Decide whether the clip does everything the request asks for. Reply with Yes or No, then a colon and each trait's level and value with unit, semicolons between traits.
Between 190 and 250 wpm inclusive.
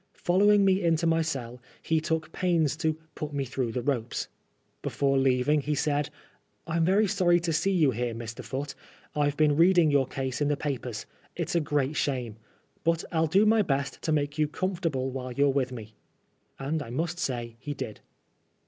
Yes: average, 195 wpm